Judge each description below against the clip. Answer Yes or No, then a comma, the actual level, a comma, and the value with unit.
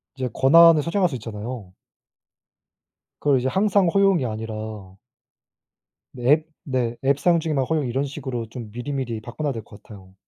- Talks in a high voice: No, low, 130 Hz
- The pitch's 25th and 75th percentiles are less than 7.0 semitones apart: Yes, average, 5.3 semitones